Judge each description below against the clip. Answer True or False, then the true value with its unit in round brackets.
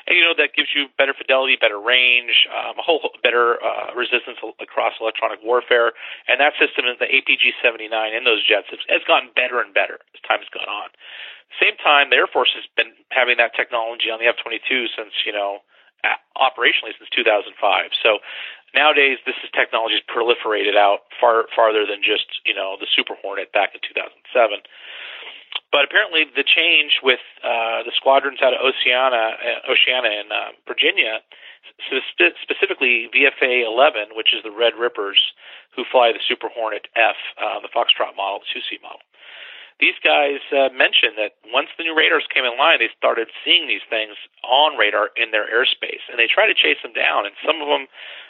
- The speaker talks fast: False (190 wpm)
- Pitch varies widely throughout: True (6.4 semitones)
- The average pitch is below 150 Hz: True (135 Hz)